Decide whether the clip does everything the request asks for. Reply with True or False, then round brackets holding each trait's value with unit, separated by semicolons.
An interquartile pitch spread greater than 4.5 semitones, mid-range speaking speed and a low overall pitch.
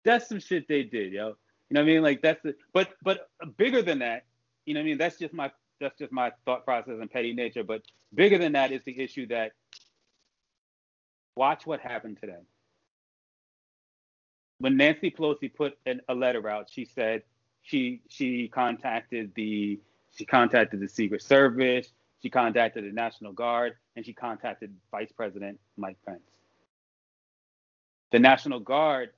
True (5.1 semitones; 165 wpm; 125 Hz)